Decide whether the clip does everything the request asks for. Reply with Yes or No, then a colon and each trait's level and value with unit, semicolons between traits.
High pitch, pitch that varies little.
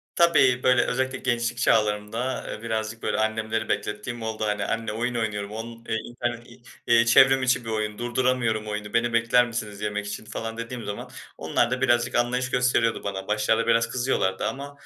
No: low, 115 Hz; narrow, 2.3 semitones